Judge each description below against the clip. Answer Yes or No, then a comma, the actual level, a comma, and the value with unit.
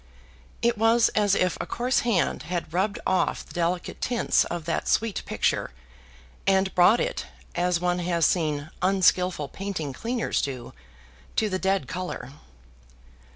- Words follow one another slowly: No, average, 145 wpm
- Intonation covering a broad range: No, average, 3.3 semitones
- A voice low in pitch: No, medium, 185 Hz